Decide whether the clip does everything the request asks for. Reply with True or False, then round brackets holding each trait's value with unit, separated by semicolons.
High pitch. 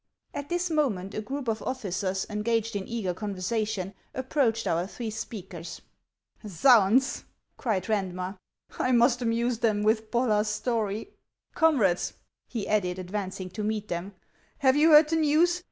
True (220 Hz)